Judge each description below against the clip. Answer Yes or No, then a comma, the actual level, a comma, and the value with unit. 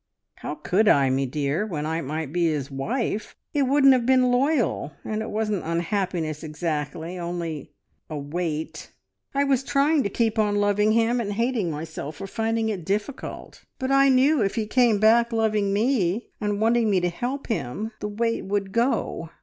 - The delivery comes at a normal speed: Yes, average, 180 wpm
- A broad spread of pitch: Yes, wide, 6.0 semitones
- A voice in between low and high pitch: No, high, 210 Hz